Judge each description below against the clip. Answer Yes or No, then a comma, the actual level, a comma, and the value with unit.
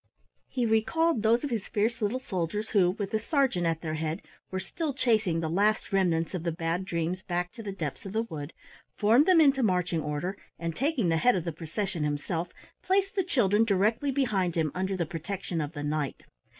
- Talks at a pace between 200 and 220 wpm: Yes, fast, 205 wpm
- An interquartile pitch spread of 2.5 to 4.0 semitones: No, wide, 5.4 semitones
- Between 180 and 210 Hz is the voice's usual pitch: Yes, high, 190 Hz